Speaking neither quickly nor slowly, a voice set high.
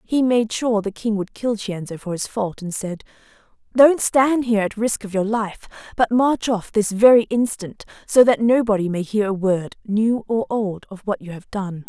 No: fast, 210 wpm; high, 215 Hz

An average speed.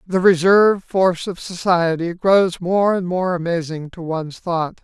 Yes: average, 160 wpm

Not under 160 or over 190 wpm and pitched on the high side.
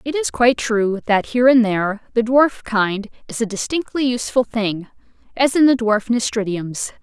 Yes: average, 180 wpm; high, 230 Hz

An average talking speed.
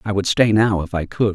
No: fast, 310 wpm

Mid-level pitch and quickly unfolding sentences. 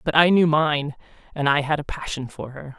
Yes: medium, 150 Hz; fast, 235 wpm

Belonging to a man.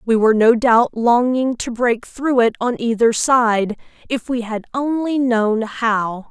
No: female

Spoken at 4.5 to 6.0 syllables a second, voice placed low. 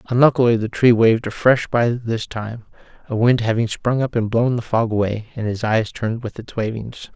Yes: 5.2 syllables/s; low, 115 Hz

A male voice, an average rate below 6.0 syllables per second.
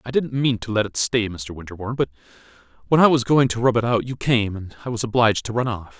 No: male; 6.4 syllables/s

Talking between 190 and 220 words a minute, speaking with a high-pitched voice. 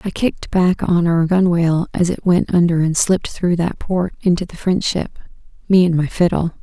No: average, 200 wpm; medium, 175 Hz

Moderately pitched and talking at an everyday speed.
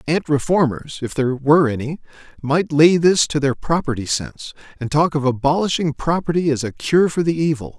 Yes: medium, 150 Hz; average, 185 wpm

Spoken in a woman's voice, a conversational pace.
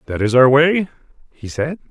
No: male; average, 190 wpm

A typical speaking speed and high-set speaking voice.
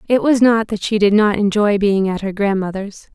No: fast, 230 wpm; high, 205 Hz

